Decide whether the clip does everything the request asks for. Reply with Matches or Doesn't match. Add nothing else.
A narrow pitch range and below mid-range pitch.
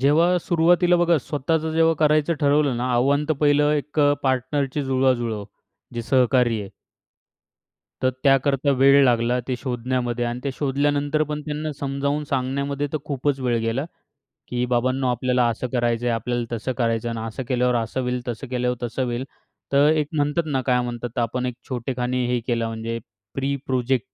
Doesn't match